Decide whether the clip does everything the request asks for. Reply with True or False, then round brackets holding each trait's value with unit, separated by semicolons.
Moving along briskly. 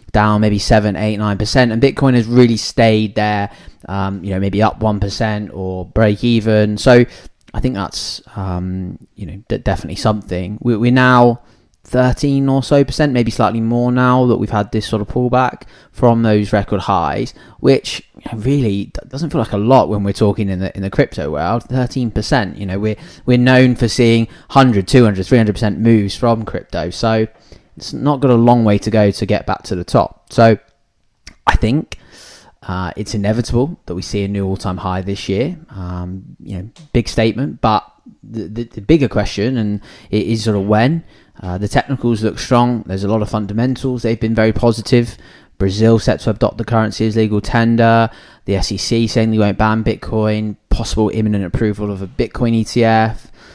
False (185 wpm)